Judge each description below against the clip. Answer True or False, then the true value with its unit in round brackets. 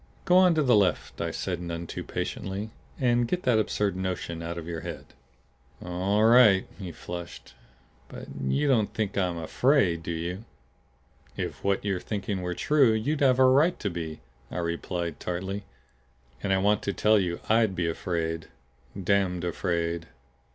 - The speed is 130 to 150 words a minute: False (165 wpm)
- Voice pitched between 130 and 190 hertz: False (95 Hz)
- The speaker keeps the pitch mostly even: False (4.2 semitones)